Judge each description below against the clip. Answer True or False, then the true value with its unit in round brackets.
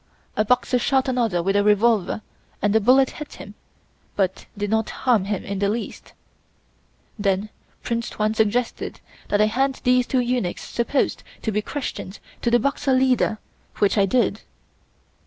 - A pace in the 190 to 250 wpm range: False (160 wpm)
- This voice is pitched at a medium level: False (220 Hz)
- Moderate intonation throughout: True (3.5 semitones)